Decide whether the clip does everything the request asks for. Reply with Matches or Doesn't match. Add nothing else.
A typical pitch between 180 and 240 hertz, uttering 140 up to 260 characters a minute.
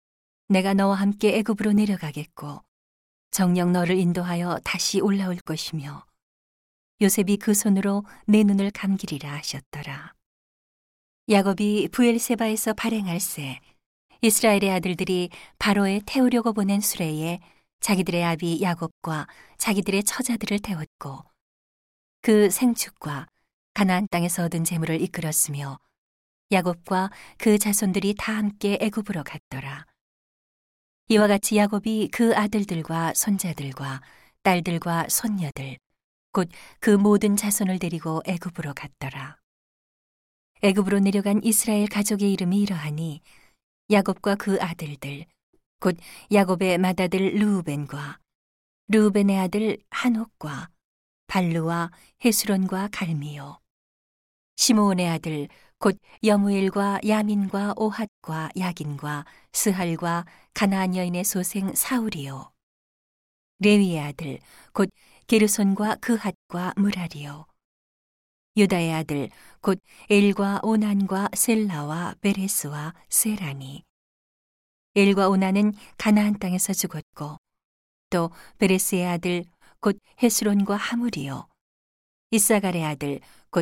Matches